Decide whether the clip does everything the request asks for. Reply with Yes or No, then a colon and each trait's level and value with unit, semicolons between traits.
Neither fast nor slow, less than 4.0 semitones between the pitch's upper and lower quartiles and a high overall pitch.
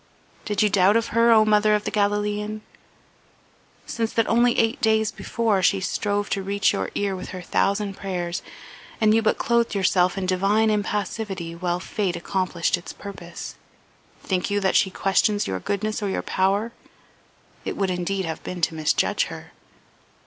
Yes: average, 170 wpm; narrow, 2.5 semitones; high, 200 Hz